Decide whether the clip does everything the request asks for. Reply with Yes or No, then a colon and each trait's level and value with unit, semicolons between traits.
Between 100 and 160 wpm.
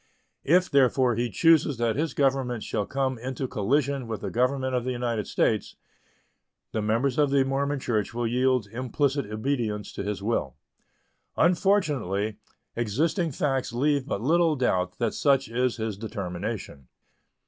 Yes: average, 150 wpm